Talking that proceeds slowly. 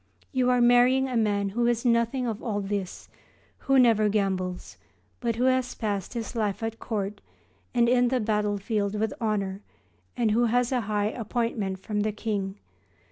No: average, 170 wpm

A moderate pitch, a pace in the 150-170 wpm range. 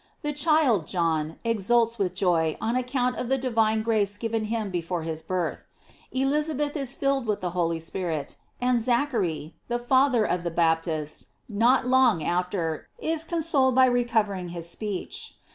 No: high, 220 Hz; average, 165 wpm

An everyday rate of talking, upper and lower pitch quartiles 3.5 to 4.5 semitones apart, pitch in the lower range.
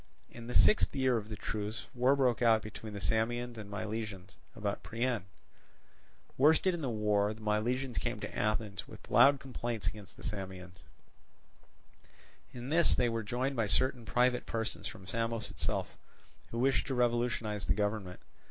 No: average, 160 wpm; average, 2.8 semitones; low, 115 Hz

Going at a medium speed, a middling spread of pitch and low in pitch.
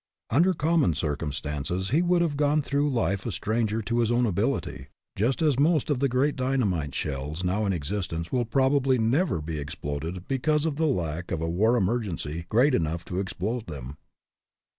No: average, 180 wpm; wide, 8.6 semitones; low, 110 Hz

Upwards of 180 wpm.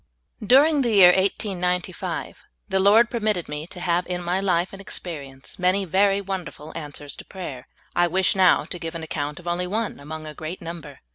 Yes: average, 195 wpm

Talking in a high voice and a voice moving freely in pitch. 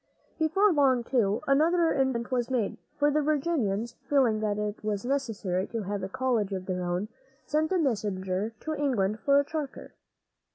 Yes: high, 240 Hz; wide, 5.8 semitones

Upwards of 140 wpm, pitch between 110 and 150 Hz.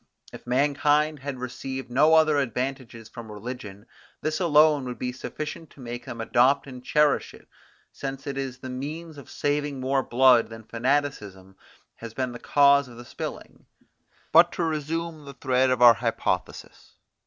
Yes: average, 160 wpm; low, 135 Hz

